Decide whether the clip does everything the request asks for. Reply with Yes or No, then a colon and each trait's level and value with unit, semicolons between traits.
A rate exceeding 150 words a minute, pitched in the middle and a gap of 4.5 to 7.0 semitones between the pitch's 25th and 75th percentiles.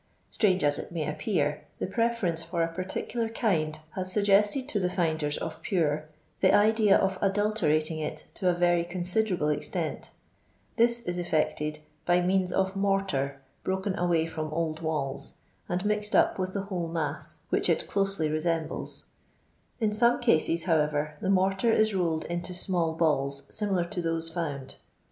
No: average, 160 wpm; medium, 175 Hz; average, 3.8 semitones